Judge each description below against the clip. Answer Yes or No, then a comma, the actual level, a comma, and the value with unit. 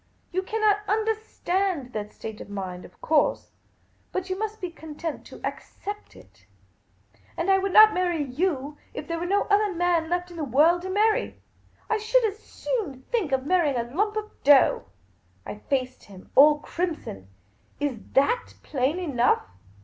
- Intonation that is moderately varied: No, wide, 6.7 semitones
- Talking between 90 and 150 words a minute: No, average, 170 wpm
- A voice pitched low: No, very high, 345 Hz